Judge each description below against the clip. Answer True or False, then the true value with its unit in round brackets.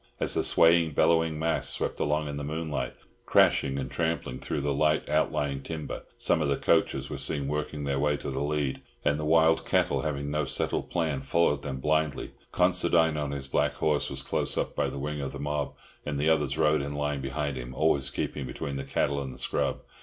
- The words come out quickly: True (215 wpm)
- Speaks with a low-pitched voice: True (75 Hz)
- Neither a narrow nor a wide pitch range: False (2.0 semitones)